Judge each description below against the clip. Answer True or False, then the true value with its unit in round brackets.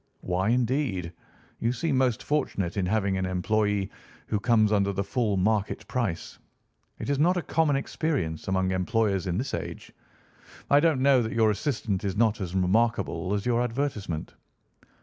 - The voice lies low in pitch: True (110 Hz)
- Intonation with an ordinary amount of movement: True (5.0 semitones)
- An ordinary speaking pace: True (165 wpm)